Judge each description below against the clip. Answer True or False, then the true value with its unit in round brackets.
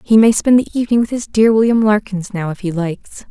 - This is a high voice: True (210 Hz)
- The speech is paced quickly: True (255 wpm)